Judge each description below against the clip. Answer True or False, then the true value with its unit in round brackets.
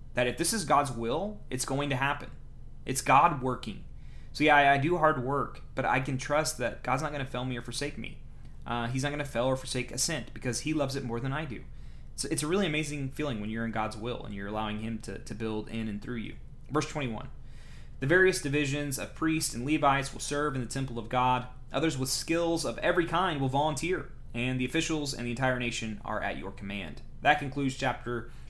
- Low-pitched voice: True (130 Hz)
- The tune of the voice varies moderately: True (3.9 semitones)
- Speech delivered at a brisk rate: True (235 wpm)